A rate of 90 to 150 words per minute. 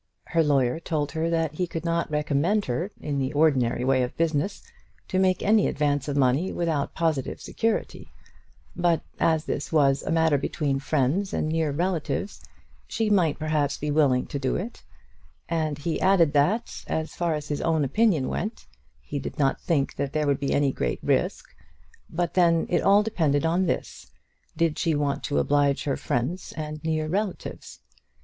No: average, 175 wpm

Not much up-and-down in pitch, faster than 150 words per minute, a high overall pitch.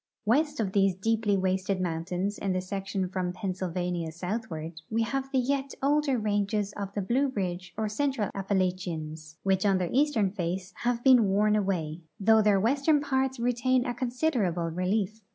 No: average, 4.5 semitones; average, 170 wpm; high, 200 Hz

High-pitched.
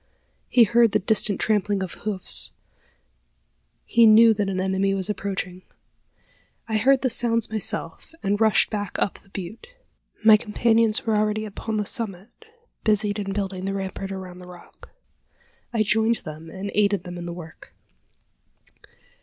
Yes: high, 205 Hz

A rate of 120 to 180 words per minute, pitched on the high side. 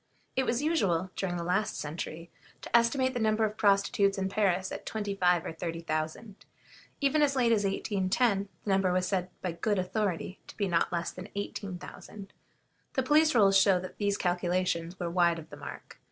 No: average, 195 wpm; high, 195 Hz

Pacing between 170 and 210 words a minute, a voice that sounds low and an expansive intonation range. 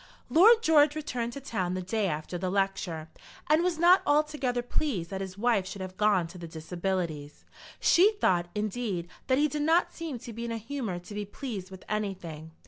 No: average, 200 wpm; high, 210 Hz; wide, 7.8 semitones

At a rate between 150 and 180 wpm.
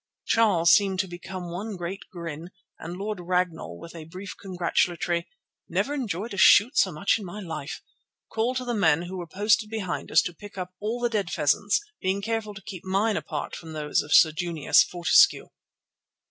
No: average, 190 wpm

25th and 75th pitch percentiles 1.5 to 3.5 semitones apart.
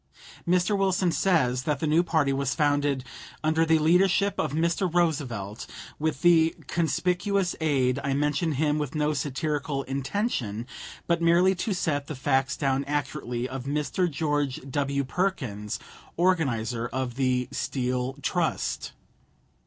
No: average, 4.0 semitones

